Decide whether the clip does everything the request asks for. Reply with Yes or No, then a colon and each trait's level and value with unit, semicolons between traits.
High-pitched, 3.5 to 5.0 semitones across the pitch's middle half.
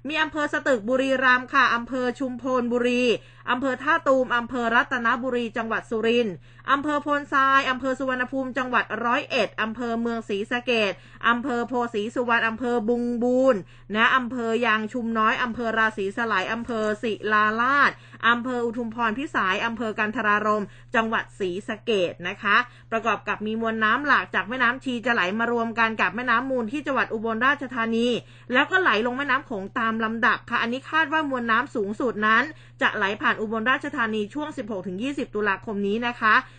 No: high, 235 Hz; average, 2.7 semitones